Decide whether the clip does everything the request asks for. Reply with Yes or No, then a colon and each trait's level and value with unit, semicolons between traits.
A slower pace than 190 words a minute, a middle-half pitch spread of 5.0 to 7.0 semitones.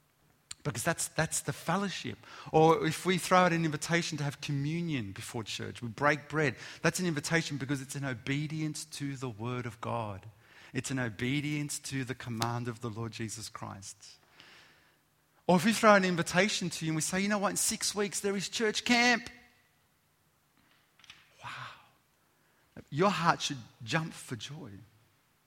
Yes: average, 170 wpm; wide, 5.5 semitones